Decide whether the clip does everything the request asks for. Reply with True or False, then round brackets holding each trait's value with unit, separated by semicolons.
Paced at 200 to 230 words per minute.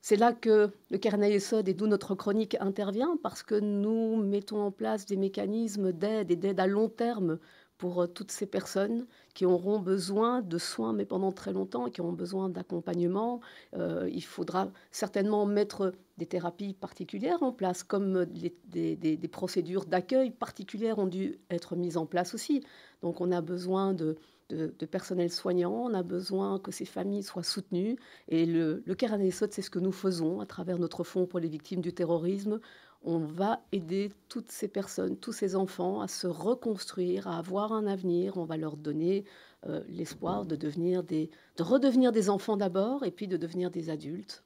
False (190 wpm)